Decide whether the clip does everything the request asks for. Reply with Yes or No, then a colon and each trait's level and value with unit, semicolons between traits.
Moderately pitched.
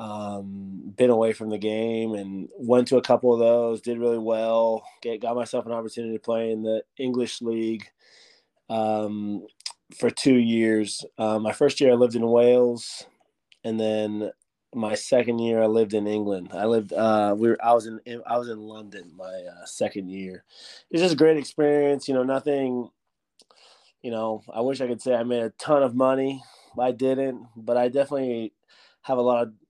No: low, 115 Hz